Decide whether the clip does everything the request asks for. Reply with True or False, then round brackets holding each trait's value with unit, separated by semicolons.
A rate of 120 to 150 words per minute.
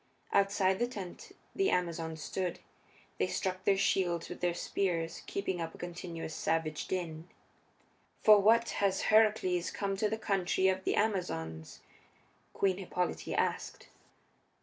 True (135 wpm)